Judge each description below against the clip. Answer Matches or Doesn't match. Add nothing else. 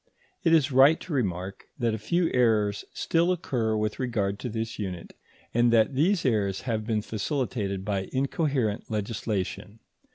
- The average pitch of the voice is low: Matches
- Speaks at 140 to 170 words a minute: Matches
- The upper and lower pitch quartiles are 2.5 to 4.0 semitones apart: Doesn't match